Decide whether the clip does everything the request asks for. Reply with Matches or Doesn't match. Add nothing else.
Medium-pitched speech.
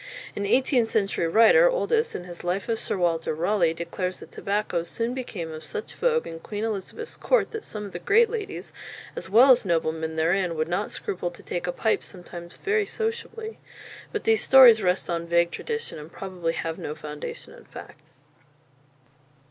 Doesn't match